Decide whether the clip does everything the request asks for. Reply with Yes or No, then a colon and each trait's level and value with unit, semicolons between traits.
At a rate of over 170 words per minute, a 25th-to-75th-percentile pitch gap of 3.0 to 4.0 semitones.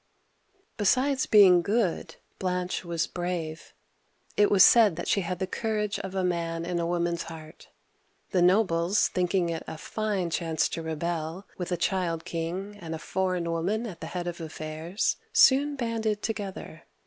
No: average, 160 wpm; average, 3.4 semitones